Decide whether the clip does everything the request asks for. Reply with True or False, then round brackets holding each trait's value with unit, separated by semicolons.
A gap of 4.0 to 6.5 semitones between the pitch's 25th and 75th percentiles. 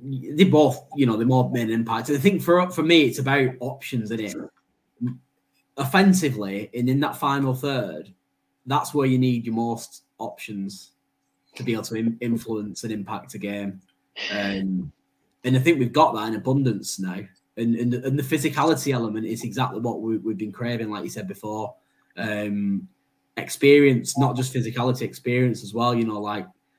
True (4.5 semitones)